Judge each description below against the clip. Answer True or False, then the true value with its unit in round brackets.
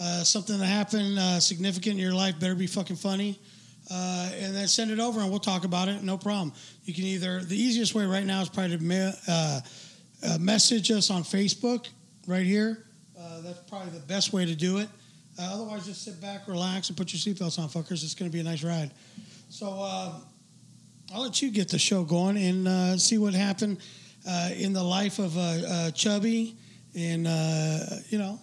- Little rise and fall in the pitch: True (2.3 semitones)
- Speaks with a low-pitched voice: False (190 Hz)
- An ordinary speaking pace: False (210 wpm)